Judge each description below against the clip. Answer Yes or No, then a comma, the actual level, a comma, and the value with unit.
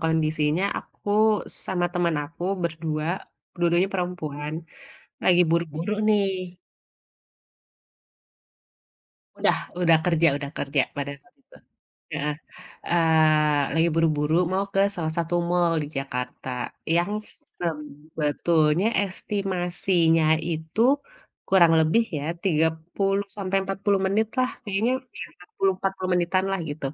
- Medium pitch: Yes, medium, 170 Hz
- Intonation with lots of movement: No, average, 3.2 semitones